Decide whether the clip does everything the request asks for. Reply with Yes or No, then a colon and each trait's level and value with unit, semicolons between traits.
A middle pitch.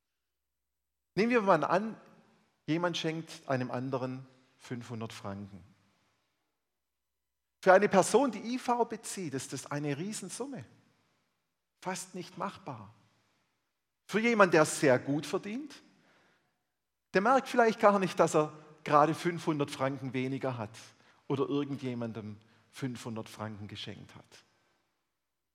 Yes: medium, 145 Hz